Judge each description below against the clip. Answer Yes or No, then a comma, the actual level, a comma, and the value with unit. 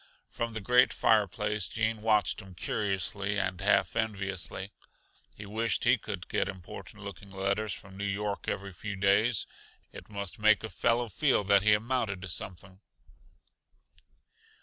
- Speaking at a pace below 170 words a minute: Yes, average, 150 wpm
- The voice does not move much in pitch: Yes, narrow, 1.8 semitones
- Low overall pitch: Yes, low, 100 Hz